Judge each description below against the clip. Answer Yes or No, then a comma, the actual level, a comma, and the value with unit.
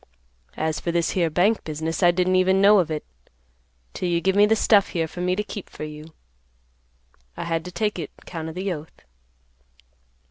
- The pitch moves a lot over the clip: No, average, 3.0 semitones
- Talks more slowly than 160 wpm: No, average, 200 wpm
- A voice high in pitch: No, medium, 175 Hz